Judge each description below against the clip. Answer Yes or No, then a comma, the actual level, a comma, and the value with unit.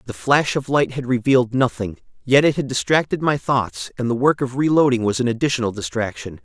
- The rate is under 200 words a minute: No, fast, 205 wpm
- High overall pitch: No, low, 130 Hz